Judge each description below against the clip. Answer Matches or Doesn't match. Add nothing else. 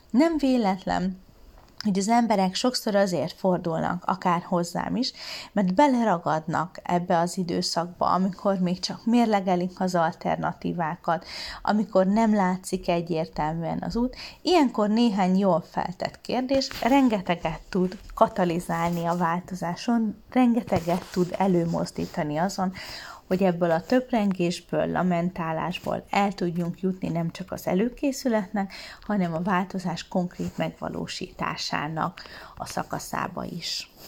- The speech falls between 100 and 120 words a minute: Matches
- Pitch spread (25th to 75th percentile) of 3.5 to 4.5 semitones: Matches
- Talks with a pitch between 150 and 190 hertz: Matches